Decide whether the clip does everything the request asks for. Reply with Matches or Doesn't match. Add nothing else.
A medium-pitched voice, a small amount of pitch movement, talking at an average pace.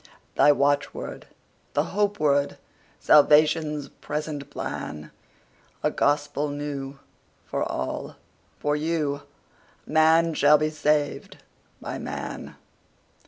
Doesn't match